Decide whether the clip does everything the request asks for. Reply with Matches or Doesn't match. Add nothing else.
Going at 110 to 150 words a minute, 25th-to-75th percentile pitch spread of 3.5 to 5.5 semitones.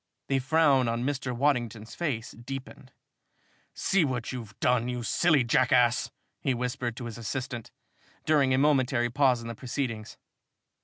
Doesn't match